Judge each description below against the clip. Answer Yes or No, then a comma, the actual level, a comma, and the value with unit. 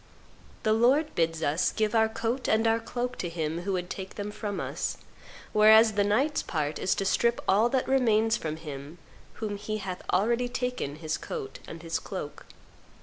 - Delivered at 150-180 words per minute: No, average, 190 wpm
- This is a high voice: Yes, high, 215 Hz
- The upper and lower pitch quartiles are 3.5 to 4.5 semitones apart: No, average, 5.2 semitones